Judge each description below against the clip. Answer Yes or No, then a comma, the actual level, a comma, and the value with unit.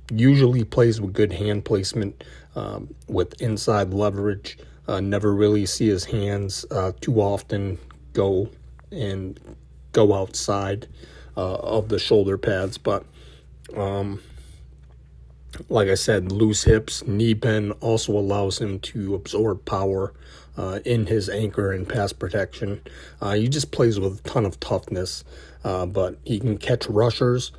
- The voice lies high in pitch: No, low, 100 Hz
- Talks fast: No, average, 140 wpm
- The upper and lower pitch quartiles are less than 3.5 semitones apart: Yes, average, 2.8 semitones